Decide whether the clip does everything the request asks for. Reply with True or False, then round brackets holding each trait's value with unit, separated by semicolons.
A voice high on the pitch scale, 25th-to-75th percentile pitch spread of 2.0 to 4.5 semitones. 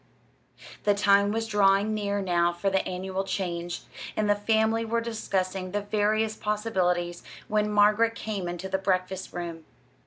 True (200 Hz; 2.5 semitones)